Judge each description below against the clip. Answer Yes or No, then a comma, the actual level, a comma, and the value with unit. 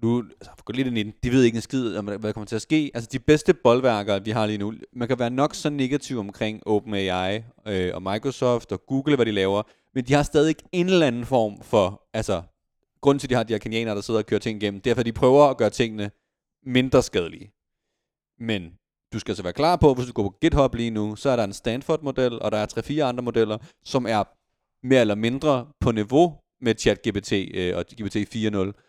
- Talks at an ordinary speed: No, fast, 230 wpm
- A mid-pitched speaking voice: No, low, 115 Hz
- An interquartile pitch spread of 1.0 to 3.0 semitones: No, average, 3.8 semitones